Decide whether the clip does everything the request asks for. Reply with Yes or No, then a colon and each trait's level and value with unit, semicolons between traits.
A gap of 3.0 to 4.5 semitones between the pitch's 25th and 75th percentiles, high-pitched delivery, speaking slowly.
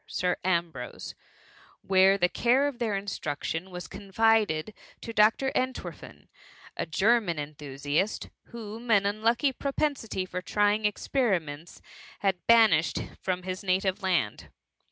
Yes: average, 4.2 semitones; high, 195 Hz; slow, 120 wpm